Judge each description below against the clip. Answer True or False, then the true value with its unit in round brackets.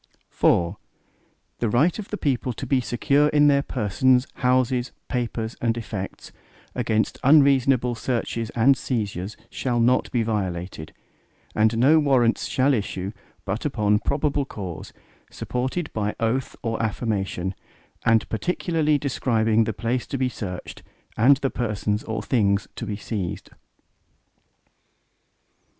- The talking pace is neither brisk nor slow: False (130 wpm)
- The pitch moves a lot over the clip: False (3.8 semitones)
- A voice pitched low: True (120 Hz)